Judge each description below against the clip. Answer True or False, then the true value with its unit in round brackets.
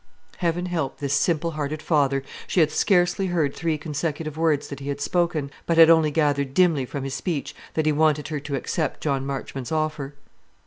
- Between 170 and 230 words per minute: True (190 wpm)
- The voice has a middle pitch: True (155 Hz)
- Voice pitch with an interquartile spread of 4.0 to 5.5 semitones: False (2.7 semitones)